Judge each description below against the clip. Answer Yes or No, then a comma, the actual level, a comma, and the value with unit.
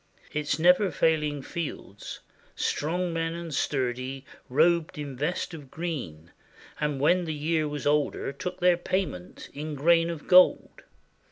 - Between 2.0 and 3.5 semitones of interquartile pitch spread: Yes, average, 3.1 semitones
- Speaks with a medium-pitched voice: Yes, medium, 155 Hz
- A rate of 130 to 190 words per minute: Yes, average, 140 wpm